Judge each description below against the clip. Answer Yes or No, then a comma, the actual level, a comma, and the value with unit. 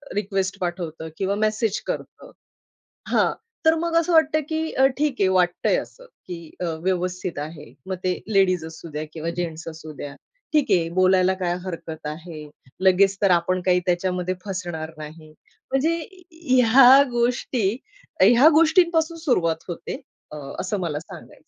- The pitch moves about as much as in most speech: No, wide, 6.9 semitones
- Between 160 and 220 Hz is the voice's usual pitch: Yes, medium, 185 Hz